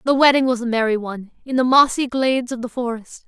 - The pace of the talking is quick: Yes, fast, 240 wpm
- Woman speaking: Yes, female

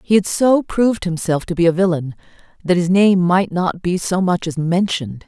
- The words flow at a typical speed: No, fast, 215 wpm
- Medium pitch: Yes, medium, 180 Hz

